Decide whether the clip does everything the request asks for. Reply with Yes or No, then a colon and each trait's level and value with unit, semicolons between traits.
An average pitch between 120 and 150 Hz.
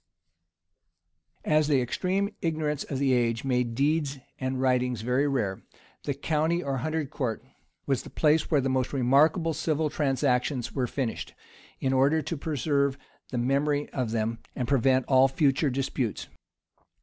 Yes: low, 135 Hz